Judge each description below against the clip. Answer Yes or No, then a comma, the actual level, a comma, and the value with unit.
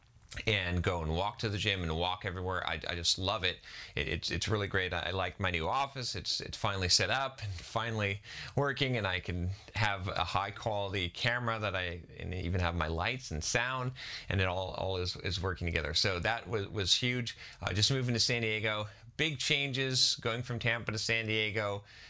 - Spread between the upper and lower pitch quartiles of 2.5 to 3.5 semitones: No, average, 4.3 semitones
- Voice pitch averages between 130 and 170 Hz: No, low, 100 Hz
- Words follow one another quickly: Yes, fast, 210 wpm